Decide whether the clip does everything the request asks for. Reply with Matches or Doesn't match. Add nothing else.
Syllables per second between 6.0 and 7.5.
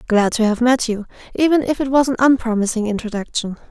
Matches